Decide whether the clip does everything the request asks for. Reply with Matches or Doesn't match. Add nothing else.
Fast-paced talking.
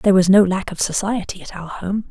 Matches